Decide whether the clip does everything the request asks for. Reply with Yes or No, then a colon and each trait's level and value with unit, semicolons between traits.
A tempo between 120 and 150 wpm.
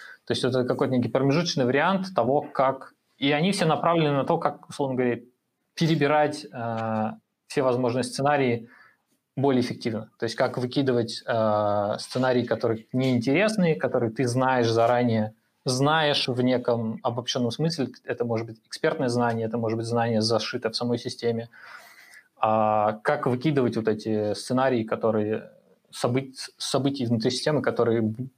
Yes: average, 140 wpm